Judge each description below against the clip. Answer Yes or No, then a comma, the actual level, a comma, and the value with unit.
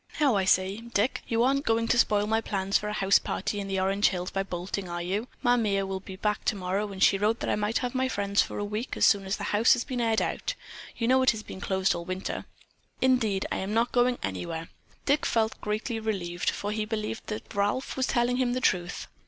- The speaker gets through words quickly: Yes, fast, 240 wpm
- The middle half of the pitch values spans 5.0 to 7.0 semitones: No, average, 3.4 semitones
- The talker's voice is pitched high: Yes, high, 210 Hz